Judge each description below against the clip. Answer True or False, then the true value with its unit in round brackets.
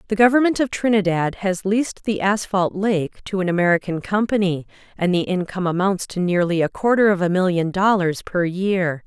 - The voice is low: False (190 Hz)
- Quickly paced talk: False (180 wpm)